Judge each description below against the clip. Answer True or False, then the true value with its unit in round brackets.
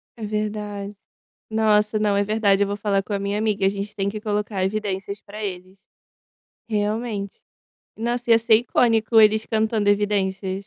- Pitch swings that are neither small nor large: False (1.5 semitones)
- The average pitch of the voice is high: True (210 Hz)